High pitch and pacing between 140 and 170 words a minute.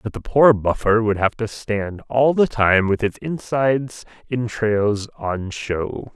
No: low, 110 Hz; average, 165 wpm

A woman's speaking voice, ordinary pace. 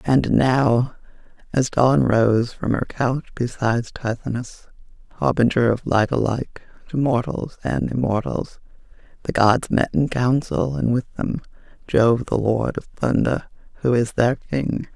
No: female; slow, 130 wpm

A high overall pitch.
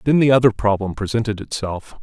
No: low, 110 Hz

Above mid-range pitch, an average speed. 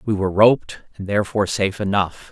No: low, 100 Hz; average, 180 wpm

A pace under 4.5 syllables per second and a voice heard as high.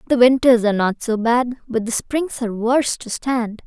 No: 5.1 syllables/s; high, 240 Hz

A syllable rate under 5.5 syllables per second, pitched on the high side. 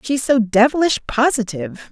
Yes: 5.0 syllables/s; high, 240 Hz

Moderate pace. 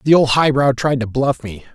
No: fast, 275 wpm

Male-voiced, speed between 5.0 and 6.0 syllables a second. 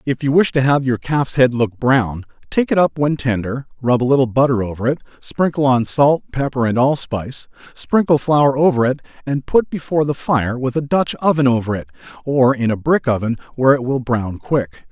Yes: male; 5.2 syllables/s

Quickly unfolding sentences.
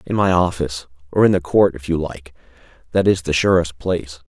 No: average, 195 wpm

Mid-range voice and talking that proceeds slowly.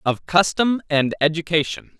Yes: medium, 165 Hz; slow, 120 wpm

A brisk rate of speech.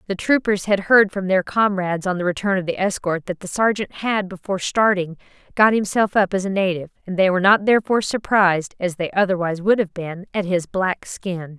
Yes: fast, 210 wpm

